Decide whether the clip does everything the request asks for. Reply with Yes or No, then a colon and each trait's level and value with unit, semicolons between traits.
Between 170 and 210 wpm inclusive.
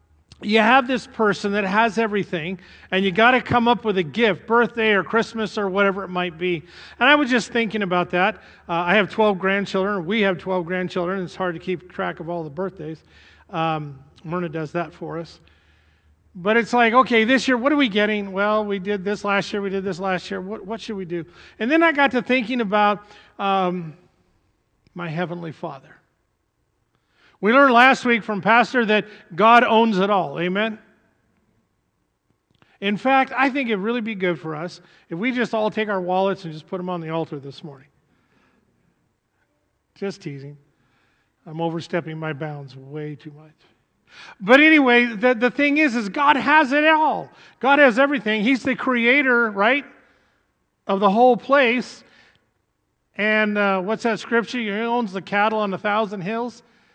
Yes: average, 185 wpm